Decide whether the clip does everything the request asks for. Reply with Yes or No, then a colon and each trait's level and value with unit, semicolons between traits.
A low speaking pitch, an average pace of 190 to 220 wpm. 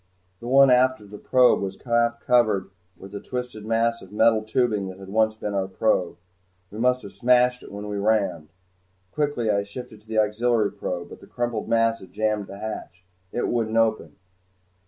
Yes: low, 110 Hz; average, 195 wpm